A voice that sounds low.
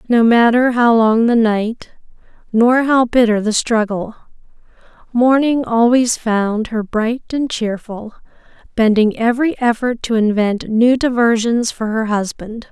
No: high, 230 Hz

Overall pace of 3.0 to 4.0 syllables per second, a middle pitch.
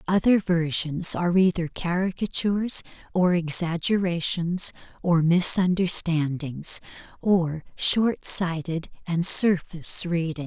Yes: 3.9 syllables/s; medium, 175 Hz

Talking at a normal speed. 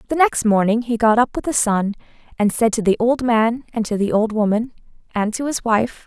No: fast, 235 wpm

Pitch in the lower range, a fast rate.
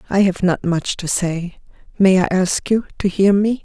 No: high, 190 Hz; fast, 215 wpm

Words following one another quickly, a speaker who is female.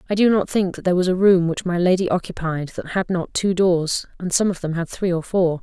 Yes: fast, 275 wpm; female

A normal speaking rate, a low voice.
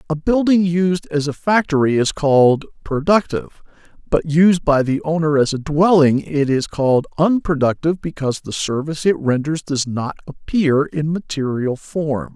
No: average, 155 wpm; medium, 155 Hz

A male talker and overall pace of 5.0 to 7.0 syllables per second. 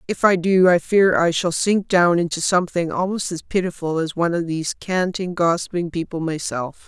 No: female; 5.3 syllables/s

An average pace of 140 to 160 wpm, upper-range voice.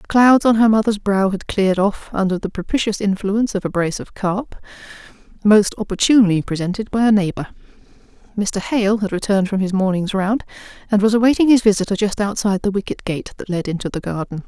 No: average, 195 wpm; high, 200 Hz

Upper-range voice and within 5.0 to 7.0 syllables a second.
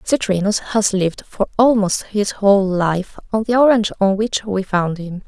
No: high, 200 Hz; 4.7 syllables/s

